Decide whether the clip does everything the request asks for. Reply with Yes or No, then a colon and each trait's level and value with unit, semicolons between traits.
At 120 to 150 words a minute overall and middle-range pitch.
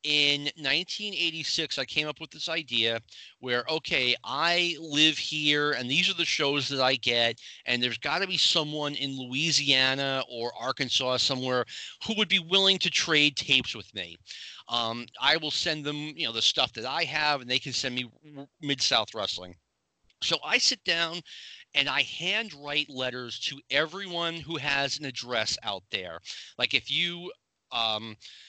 No: average, 170 wpm; medium, 145 Hz